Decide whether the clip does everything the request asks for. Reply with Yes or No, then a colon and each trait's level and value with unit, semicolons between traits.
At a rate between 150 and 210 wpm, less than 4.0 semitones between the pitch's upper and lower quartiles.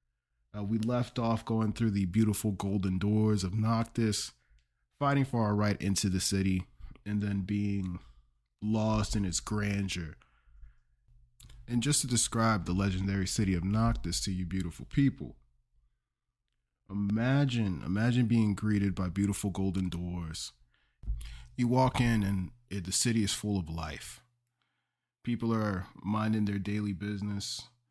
No: average, 140 wpm; average, 3.6 semitones